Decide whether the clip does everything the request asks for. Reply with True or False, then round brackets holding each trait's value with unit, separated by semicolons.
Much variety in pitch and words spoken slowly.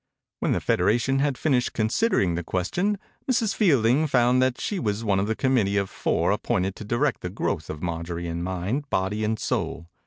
False (6.3 semitones; 195 wpm)